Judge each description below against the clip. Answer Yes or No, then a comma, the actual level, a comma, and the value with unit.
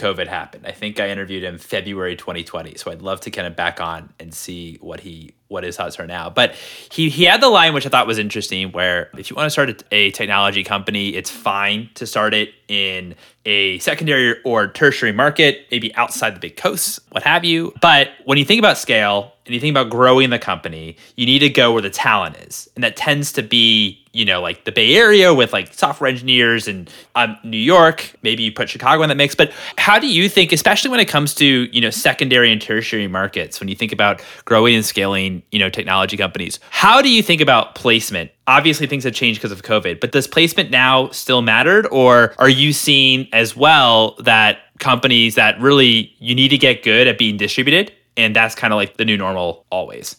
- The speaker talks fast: Yes, fast, 220 wpm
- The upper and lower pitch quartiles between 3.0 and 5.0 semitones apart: No, wide, 5.6 semitones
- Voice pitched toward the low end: Yes, low, 115 Hz